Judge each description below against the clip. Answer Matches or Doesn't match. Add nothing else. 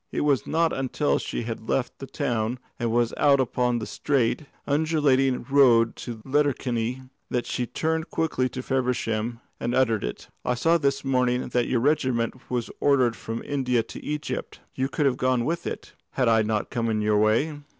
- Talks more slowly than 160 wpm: Doesn't match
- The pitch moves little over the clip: Doesn't match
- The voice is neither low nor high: Doesn't match